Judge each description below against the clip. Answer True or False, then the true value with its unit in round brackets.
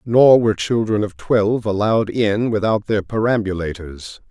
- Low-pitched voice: True (105 Hz)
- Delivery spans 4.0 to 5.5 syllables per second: True (4.8 syllables/s)